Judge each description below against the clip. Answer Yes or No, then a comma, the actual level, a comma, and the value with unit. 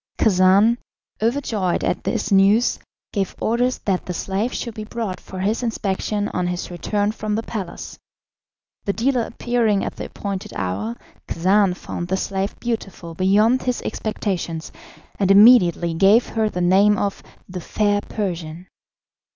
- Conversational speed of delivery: Yes, average, 145 wpm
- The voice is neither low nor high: No, high, 200 Hz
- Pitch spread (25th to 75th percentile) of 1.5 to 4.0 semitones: Yes, average, 3.2 semitones